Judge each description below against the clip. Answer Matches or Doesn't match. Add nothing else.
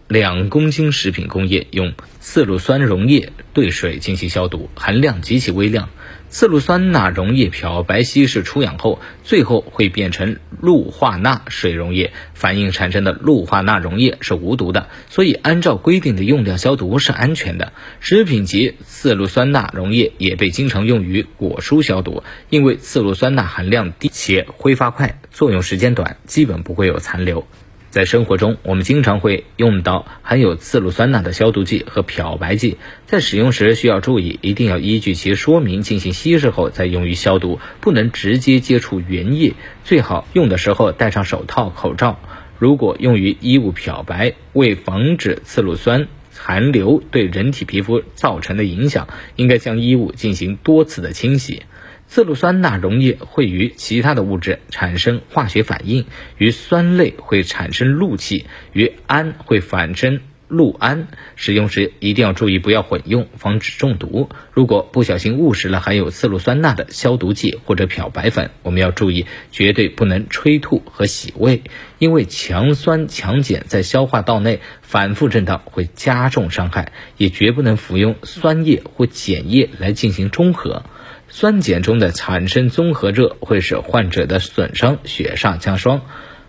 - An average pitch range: Doesn't match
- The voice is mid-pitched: Doesn't match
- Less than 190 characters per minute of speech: Doesn't match